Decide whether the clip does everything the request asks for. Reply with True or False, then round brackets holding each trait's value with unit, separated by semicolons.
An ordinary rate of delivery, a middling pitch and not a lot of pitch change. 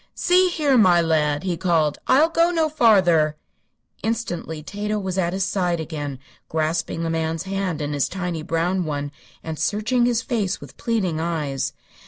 False (165 wpm; 175 Hz; 5.0 semitones)